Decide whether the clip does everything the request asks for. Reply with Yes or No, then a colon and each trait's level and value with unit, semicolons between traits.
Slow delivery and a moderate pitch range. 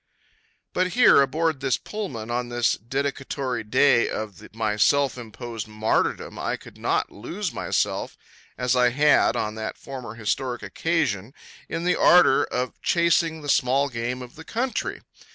No: average, 155 wpm; average, 4.1 semitones